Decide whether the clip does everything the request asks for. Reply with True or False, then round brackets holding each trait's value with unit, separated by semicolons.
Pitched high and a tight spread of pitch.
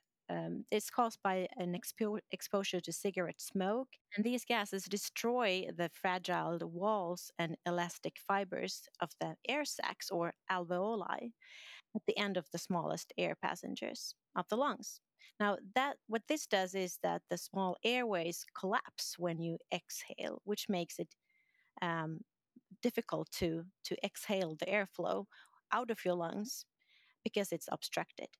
False (195 Hz; 4.4 semitones)